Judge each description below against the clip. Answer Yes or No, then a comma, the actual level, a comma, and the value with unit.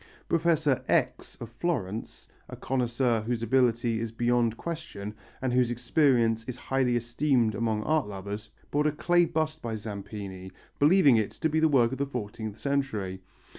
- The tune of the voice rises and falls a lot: No, average, 4.4 semitones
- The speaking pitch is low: Yes, low, 120 Hz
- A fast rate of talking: No, average, 155 wpm